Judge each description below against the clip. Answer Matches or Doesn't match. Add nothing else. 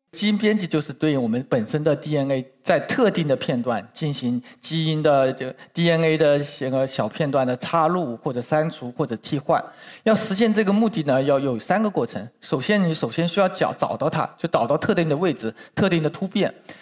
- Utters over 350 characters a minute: Doesn't match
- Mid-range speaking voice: Matches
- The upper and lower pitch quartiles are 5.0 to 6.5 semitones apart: Matches